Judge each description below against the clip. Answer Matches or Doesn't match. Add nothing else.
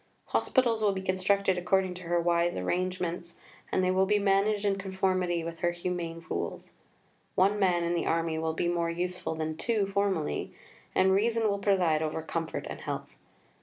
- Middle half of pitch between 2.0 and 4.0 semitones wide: Matches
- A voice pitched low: Doesn't match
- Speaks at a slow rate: Doesn't match